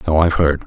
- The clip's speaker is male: Yes, male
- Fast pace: Yes, fast, 270 wpm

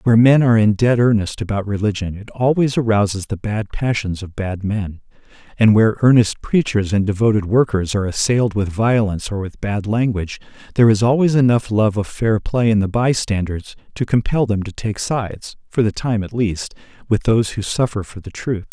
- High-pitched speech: No, low, 110 Hz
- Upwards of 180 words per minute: Yes, average, 195 wpm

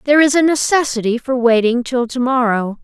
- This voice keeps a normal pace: Yes, average, 190 wpm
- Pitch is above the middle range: Yes, very high, 250 Hz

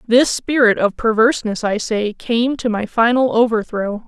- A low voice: No, high, 230 Hz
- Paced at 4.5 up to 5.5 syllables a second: Yes, 4.6 syllables/s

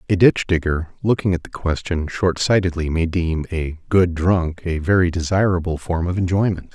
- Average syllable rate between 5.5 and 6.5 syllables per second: No, 4.9 syllables/s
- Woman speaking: No, male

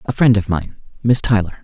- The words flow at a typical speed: Yes, average, 185 wpm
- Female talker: No, male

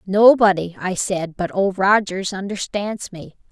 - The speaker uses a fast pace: No, slow, 135 wpm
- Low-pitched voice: No, high, 190 Hz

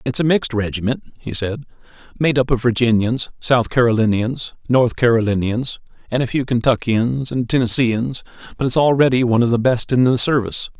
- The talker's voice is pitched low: Yes, low, 120 Hz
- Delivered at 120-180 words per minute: Yes, average, 165 wpm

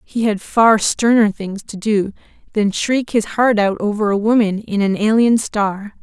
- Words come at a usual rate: Yes, average, 190 wpm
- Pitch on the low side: No, high, 210 Hz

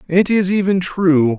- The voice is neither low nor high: Yes, medium, 175 Hz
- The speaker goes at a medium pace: Yes, average, 175 wpm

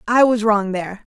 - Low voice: No, high, 215 Hz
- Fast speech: Yes, fast, 215 wpm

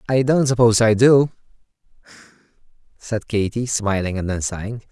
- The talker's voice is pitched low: Yes, low, 115 Hz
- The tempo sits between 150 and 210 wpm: No, slow, 135 wpm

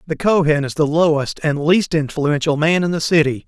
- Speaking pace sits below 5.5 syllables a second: Yes, 5.1 syllables/s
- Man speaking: Yes, male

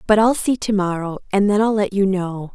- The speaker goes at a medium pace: No, fast, 260 wpm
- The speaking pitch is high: Yes, high, 200 Hz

